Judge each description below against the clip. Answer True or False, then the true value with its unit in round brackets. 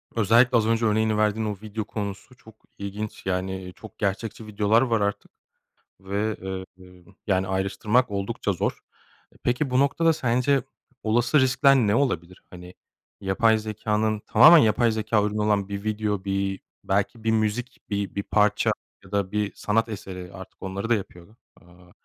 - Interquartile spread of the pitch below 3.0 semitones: True (2.5 semitones)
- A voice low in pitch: True (105 Hz)